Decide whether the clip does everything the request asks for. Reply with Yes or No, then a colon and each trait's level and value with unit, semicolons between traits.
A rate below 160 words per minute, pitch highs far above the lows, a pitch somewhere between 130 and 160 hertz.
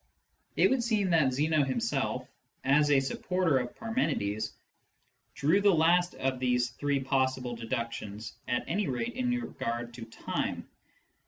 Yes: average, 140 wpm; wide, 6.5 semitones; low, 135 Hz